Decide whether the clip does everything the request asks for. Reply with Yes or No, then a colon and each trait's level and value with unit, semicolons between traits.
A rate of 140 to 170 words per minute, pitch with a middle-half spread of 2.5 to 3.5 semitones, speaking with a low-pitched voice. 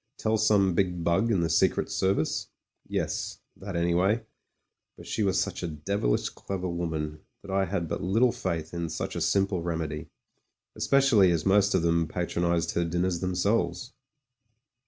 Yes: average, 160 wpm; average, 2.9 semitones; very low, 90 Hz